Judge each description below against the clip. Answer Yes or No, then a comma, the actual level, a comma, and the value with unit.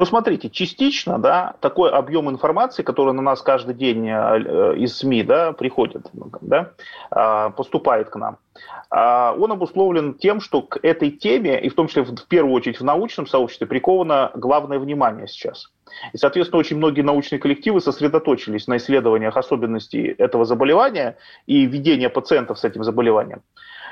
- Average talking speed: Yes, average, 150 wpm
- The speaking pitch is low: No, medium, 145 Hz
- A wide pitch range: Yes, wide, 5.7 semitones